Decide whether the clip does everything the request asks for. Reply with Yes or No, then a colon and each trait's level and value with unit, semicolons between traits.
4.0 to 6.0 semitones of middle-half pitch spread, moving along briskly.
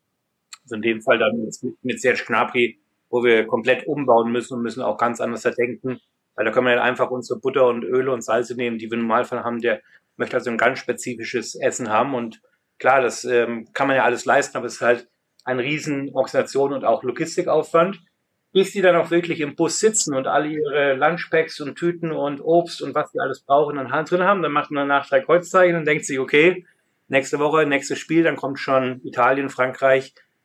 Yes: average, 4.3 semitones; fast, 210 wpm